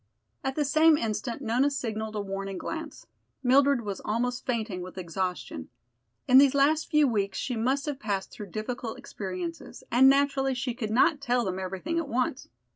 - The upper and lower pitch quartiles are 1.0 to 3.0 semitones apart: No, wide, 5.4 semitones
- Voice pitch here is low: No, high, 245 Hz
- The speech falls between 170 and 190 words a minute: Yes, average, 175 wpm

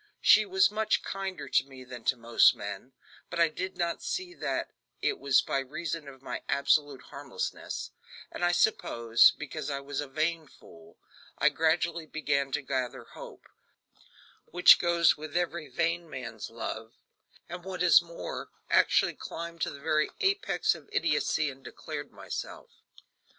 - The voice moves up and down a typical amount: Yes, average, 4.2 semitones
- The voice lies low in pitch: No, medium, 155 Hz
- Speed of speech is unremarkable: Yes, average, 155 wpm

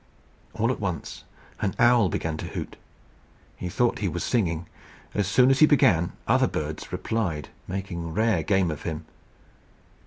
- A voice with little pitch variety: No, wide, 5.4 semitones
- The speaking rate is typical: Yes, average, 155 wpm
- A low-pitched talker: Yes, very low, 95 Hz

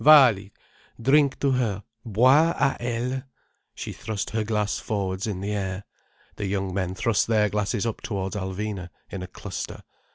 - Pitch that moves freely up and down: No, average, 3.5 semitones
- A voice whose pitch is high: No, low, 105 Hz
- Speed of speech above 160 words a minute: No, average, 155 wpm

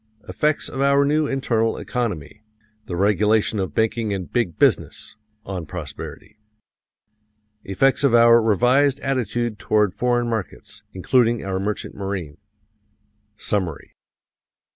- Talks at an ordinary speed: No, slow, 115 wpm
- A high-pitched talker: No, low, 110 Hz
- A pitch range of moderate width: Yes, average, 4.2 semitones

